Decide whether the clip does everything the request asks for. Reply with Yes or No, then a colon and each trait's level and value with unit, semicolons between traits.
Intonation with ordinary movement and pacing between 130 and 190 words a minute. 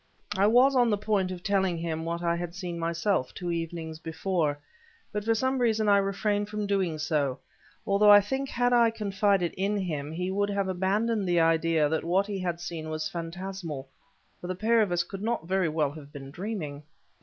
No: average, 3.8 semitones; average, 200 wpm